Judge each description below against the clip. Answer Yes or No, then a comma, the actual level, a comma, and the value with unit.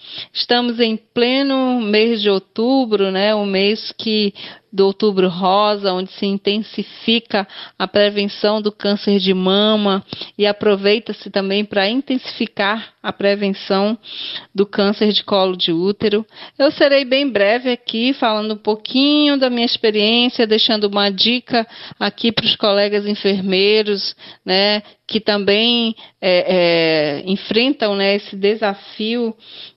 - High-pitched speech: Yes, high, 210 Hz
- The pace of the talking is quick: No, average, 130 wpm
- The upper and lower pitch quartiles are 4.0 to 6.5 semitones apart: No, narrow, 2.4 semitones